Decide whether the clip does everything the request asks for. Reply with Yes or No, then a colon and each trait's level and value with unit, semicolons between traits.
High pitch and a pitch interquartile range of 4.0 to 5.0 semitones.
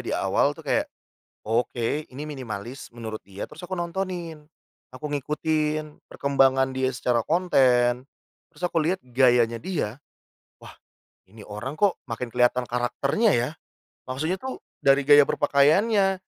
No: low, 135 Hz; average, 4.6 semitones